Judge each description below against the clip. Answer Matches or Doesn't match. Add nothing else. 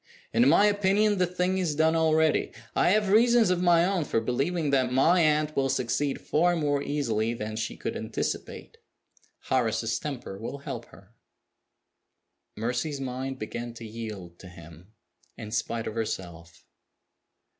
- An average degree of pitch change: Doesn't match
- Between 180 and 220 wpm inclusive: Doesn't match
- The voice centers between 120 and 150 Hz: Matches